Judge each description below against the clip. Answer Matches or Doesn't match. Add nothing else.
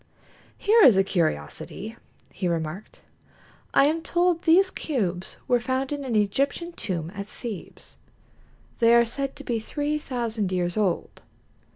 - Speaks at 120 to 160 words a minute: Matches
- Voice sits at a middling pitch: Doesn't match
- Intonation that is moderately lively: Doesn't match